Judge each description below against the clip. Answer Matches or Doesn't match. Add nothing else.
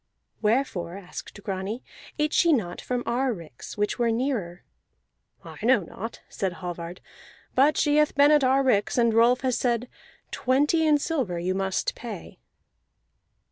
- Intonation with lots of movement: Matches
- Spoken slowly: Doesn't match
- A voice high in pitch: Matches